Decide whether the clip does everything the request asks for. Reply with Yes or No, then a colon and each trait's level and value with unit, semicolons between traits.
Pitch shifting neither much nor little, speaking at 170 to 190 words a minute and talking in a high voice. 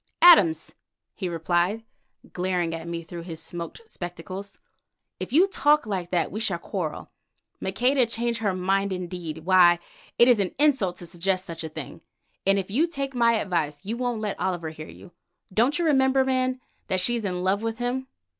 No: wide, 5.7 semitones; average, 180 wpm; high, 195 Hz